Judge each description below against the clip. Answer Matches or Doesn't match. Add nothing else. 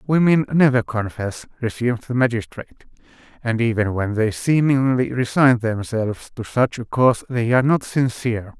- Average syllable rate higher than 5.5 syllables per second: Doesn't match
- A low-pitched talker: Matches